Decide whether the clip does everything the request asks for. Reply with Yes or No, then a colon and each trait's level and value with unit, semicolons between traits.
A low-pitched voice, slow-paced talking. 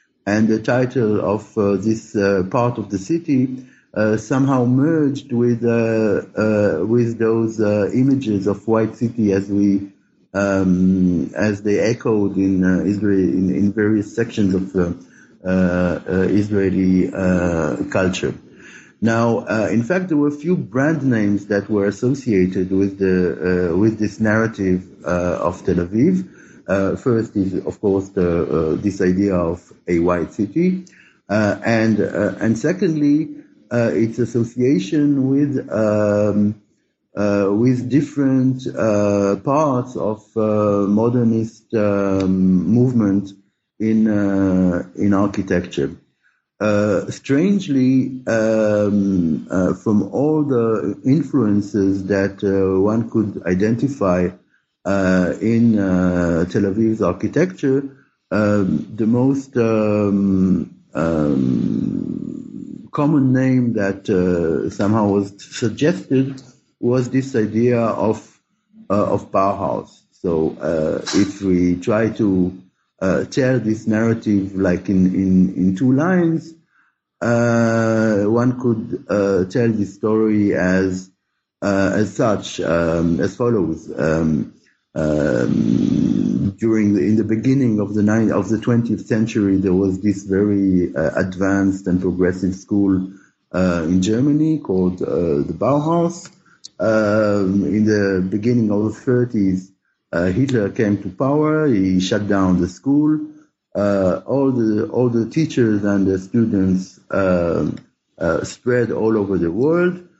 Yes: low, 105 Hz; slow, 130 wpm